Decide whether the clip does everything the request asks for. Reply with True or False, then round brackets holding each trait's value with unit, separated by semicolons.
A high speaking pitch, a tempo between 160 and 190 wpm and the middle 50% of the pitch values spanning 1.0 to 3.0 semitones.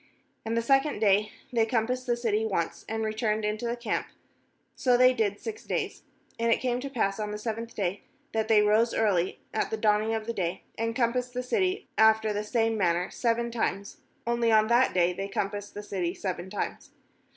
False (220 Hz; 205 wpm; 2.4 semitones)